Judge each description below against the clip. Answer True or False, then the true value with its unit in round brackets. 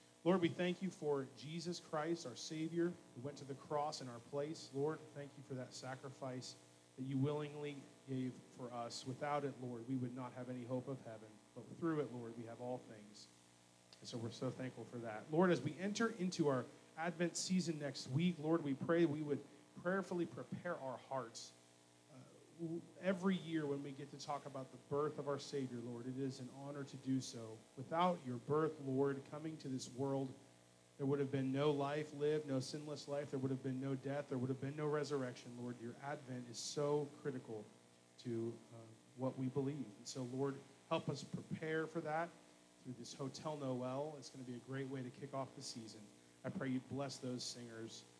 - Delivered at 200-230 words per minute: True (205 wpm)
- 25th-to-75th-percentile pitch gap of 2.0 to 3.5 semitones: True (3.2 semitones)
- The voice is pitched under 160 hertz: True (135 Hz)